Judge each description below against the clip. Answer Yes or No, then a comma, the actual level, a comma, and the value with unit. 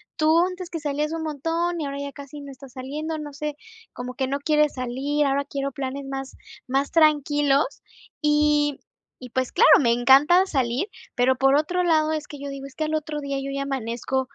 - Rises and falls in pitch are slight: Yes, narrow, 2.2 semitones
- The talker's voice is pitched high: Yes, very high, 285 Hz